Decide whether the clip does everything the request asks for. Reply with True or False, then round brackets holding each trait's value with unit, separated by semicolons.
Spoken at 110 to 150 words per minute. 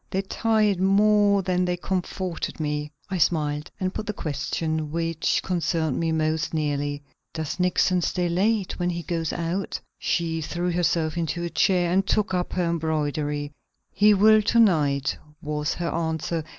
False (160 wpm)